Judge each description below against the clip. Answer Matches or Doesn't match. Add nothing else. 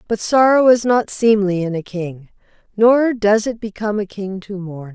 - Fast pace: Doesn't match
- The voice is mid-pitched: Doesn't match